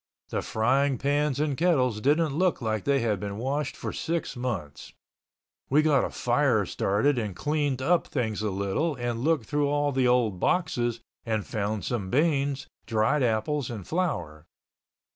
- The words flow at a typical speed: Yes, average, 160 wpm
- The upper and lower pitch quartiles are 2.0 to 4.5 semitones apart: No, average, 5.1 semitones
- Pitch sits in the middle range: No, low, 130 Hz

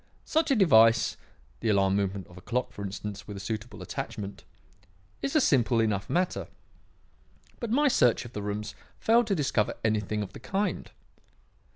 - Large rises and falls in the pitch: Yes, wide, 8.6 semitones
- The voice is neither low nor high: No, low, 110 Hz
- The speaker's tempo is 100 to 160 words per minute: No, average, 170 wpm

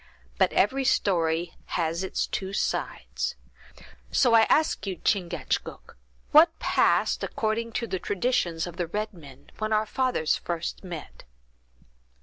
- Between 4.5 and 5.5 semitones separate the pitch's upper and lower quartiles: Yes, average, 4.9 semitones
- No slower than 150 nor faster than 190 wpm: No, slow, 135 wpm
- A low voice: No, high, 195 Hz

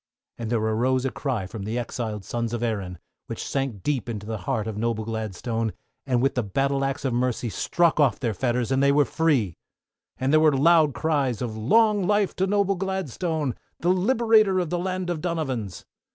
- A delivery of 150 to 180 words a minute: No, average, 195 wpm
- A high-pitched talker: No, low, 130 Hz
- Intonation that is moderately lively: No, wide, 6.5 semitones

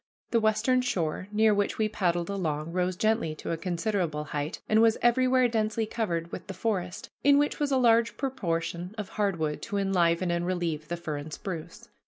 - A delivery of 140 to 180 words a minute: No, average, 195 wpm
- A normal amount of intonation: Yes, average, 4.8 semitones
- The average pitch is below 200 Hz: Yes, high, 190 Hz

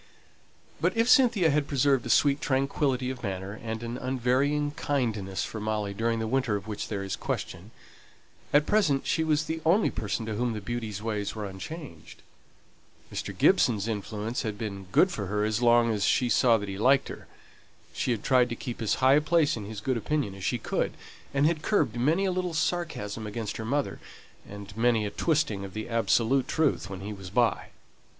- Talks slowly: No, average, 200 wpm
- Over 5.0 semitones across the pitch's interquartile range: Yes, wide, 5.4 semitones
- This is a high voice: No, low, 115 Hz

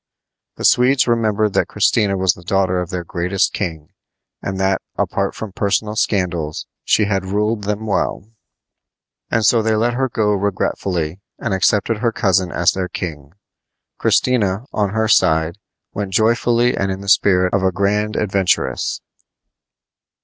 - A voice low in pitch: Yes, low, 100 Hz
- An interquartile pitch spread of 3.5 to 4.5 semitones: No, average, 2.9 semitones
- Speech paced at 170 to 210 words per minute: No, average, 150 wpm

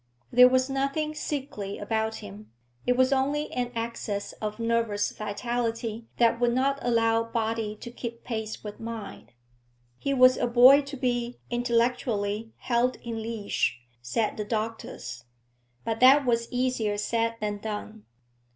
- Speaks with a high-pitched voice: Yes, high, 230 Hz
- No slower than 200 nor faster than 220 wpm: No, average, 140 wpm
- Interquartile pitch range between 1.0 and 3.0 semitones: Yes, narrow, 2.5 semitones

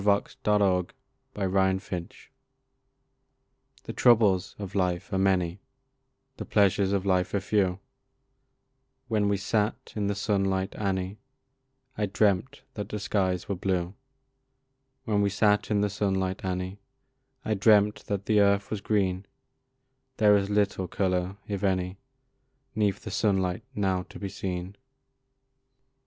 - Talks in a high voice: No, low, 100 Hz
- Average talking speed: No, slow, 130 wpm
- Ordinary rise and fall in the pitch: No, narrow, 1.7 semitones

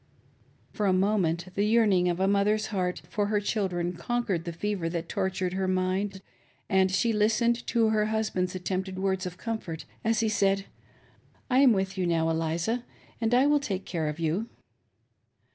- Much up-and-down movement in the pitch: No, average, 3.2 semitones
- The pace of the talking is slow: No, average, 180 wpm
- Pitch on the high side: Yes, high, 195 Hz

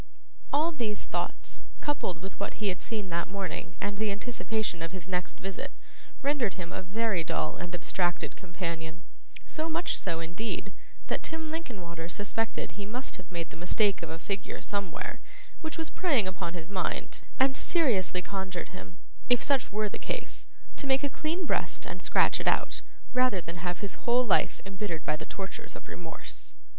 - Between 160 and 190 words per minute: Yes, average, 180 wpm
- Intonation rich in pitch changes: Yes, wide, 5.7 semitones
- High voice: Yes, high, 195 Hz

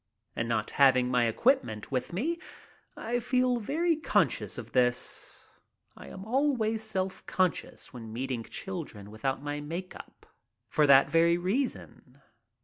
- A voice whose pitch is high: No, medium, 170 Hz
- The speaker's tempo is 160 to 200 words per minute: No, average, 140 wpm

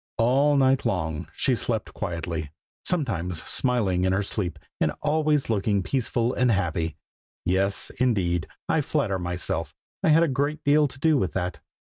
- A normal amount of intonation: No, wide, 7.5 semitones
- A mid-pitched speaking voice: No, low, 105 Hz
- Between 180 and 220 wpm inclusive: No, average, 155 wpm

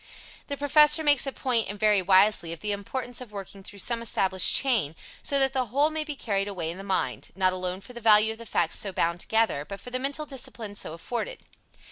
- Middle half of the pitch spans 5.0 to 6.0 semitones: Yes, average, 5.3 semitones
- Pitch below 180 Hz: No, high, 215 Hz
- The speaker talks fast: Yes, fast, 230 wpm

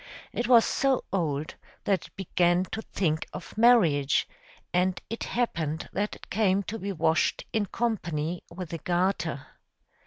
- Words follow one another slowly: No, average, 150 wpm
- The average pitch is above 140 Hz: Yes, medium, 185 Hz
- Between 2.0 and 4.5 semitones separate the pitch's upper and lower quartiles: No, average, 5.0 semitones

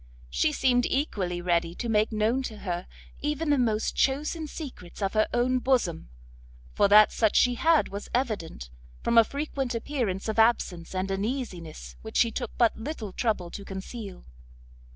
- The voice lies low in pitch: No, high, 220 Hz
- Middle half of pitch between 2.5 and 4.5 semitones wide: No, average, 5.0 semitones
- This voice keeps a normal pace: Yes, average, 165 wpm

